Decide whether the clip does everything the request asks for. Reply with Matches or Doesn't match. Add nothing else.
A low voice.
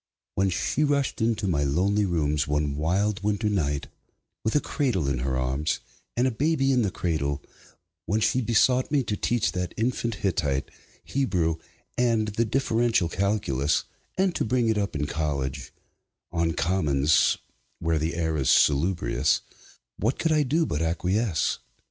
Matches